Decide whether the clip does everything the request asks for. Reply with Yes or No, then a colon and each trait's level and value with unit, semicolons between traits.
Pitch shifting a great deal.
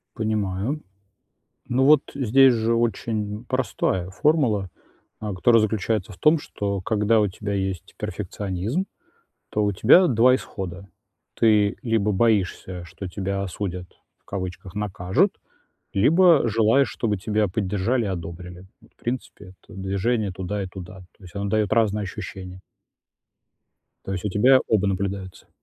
No: average, 3.3 semitones